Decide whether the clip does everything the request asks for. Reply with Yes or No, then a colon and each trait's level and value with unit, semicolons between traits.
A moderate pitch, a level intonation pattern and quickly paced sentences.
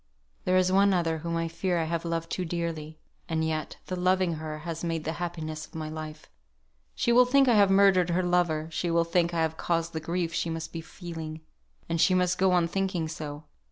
Yes: medium, 170 Hz; narrow, 2.2 semitones; fast, 225 wpm